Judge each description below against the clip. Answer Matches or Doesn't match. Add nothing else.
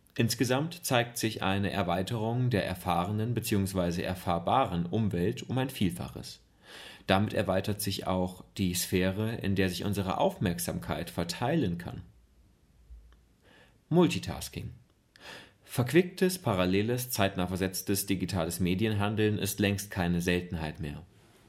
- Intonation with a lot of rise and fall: Doesn't match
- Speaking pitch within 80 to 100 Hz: Matches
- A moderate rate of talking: Doesn't match